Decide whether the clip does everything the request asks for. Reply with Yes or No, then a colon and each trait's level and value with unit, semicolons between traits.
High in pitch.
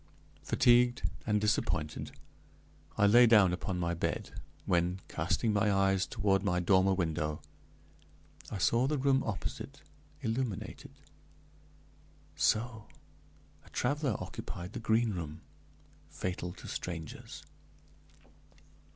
No: low, 100 Hz